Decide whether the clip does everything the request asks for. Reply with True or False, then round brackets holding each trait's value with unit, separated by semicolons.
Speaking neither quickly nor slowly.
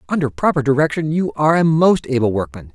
True (195 wpm)